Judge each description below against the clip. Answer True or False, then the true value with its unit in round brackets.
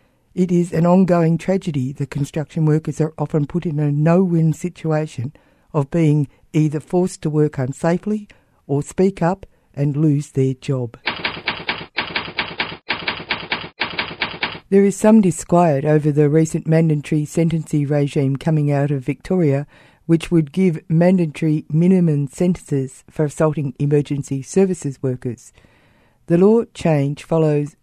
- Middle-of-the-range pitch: True (155 Hz)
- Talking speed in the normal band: False (125 wpm)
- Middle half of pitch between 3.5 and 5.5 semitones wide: False (3.0 semitones)